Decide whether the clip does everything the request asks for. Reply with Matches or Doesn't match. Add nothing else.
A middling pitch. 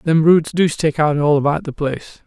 Matches